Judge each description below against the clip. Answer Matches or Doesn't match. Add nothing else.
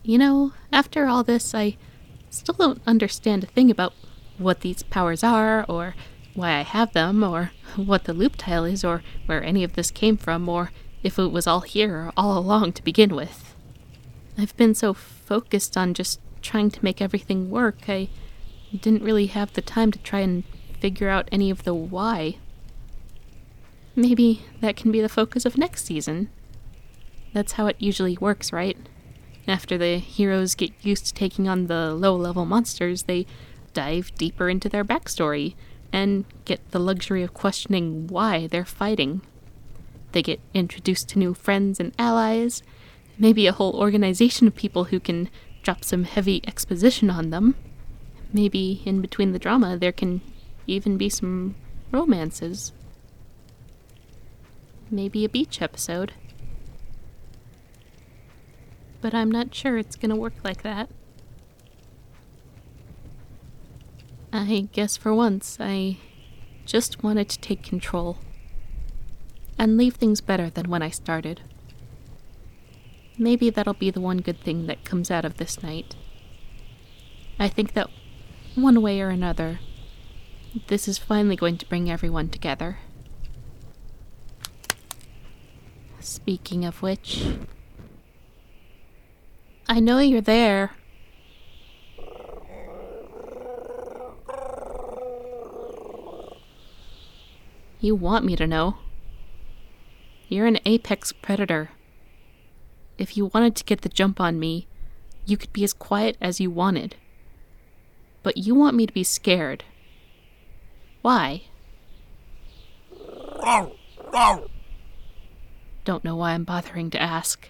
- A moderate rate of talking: Doesn't match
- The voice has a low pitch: Doesn't match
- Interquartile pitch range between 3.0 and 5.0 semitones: Matches